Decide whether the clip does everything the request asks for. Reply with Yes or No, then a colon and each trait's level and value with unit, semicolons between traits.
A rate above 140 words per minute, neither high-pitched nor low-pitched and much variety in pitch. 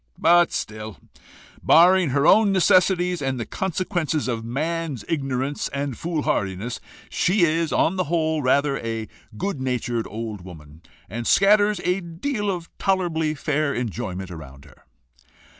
No: slow, 135 wpm; medium, 150 Hz; wide, 7.1 semitones